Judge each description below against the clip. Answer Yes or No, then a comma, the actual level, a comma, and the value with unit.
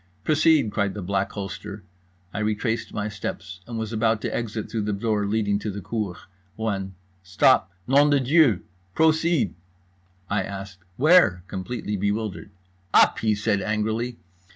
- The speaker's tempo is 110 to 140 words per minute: No, average, 150 wpm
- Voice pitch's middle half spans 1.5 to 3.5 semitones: Yes, average, 2.7 semitones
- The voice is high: No, low, 105 Hz